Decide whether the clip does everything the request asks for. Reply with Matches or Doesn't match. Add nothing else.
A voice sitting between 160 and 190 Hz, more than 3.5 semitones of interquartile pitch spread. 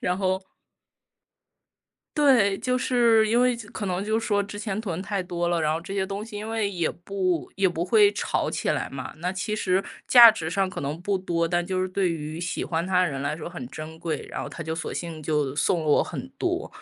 Matches